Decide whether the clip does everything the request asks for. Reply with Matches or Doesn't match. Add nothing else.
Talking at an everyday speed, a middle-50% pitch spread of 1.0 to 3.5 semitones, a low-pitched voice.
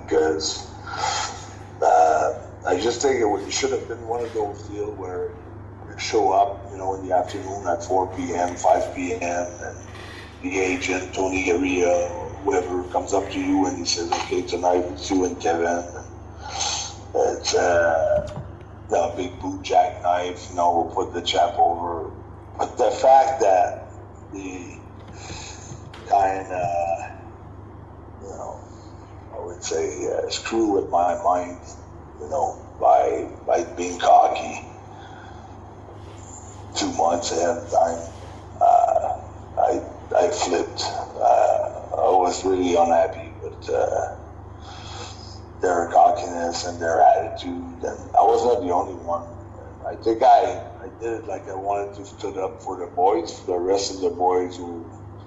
Doesn't match